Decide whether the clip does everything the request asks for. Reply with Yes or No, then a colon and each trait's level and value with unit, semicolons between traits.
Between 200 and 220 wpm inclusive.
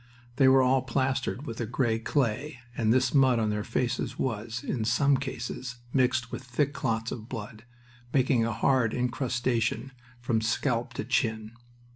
No: average, 160 wpm